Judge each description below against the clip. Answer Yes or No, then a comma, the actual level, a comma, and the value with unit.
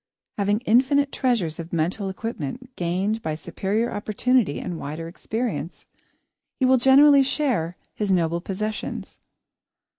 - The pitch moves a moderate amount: No, wide, 6.7 semitones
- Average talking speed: No, slow, 120 wpm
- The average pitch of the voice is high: Yes, high, 210 Hz